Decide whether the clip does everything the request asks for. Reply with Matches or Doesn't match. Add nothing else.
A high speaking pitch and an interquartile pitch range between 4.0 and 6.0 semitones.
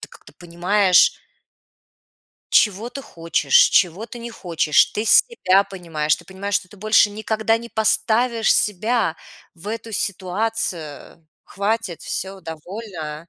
Matches